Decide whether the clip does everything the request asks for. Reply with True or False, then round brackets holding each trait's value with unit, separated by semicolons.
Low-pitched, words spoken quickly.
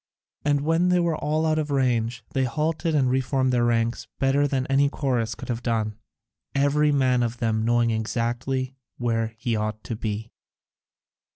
False (125 Hz; 170 wpm)